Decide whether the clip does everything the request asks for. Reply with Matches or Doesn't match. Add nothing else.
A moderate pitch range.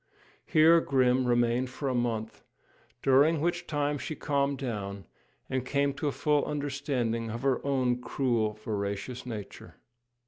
Matches